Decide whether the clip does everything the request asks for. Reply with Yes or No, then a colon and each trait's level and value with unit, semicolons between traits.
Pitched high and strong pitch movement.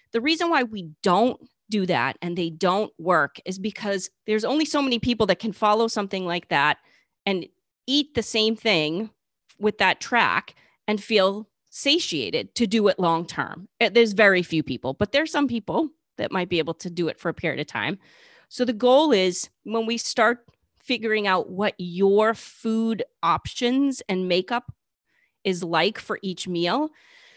No: high, 210 Hz; average, 4.8 semitones